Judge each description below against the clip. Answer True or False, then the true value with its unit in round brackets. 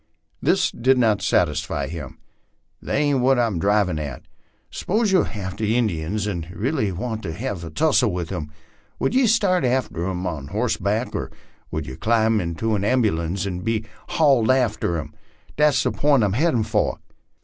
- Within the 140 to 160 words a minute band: False (170 wpm)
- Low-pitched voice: True (105 Hz)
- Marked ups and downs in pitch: True (6.5 semitones)